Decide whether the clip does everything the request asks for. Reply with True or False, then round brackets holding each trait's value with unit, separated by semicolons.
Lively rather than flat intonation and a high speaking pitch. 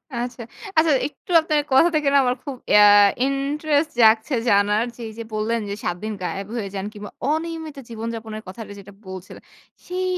True (5.8 semitones; 230 Hz)